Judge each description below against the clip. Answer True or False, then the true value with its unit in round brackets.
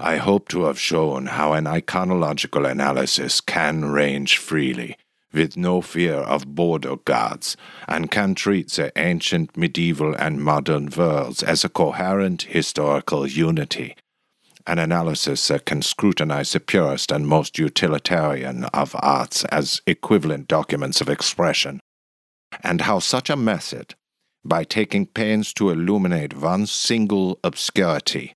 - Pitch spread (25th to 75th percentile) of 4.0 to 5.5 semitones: True (4.6 semitones)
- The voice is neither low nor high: False (80 Hz)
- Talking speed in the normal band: False (130 wpm)